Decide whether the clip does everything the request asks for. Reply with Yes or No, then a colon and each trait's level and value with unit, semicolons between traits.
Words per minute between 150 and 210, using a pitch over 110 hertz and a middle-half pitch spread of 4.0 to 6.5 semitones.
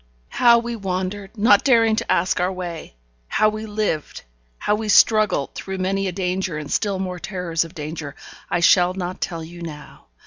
No: average, 180 wpm; medium, 185 Hz; average, 3.5 semitones